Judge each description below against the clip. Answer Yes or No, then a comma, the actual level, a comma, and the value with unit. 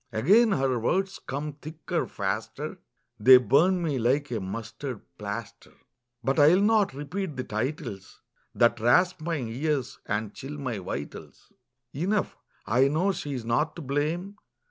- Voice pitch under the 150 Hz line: Yes, medium, 140 Hz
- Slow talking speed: No, average, 145 wpm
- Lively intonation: Yes, wide, 6.0 semitones